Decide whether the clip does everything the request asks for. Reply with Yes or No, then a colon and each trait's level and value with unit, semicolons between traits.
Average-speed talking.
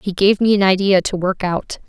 No: fast, 255 wpm